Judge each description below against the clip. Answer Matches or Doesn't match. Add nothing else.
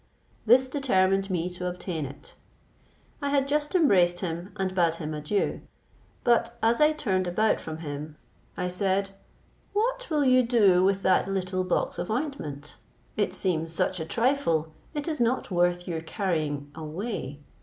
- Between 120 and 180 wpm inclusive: Matches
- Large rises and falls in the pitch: Matches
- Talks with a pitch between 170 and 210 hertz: Matches